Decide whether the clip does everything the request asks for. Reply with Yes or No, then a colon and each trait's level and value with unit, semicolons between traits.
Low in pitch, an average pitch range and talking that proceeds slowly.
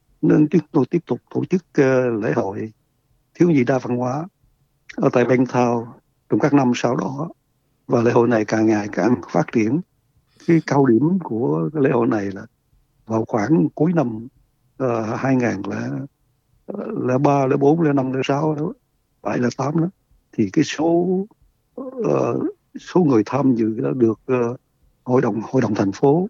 Yes: low, 130 Hz; average, 4.1 semitones; slow, 160 wpm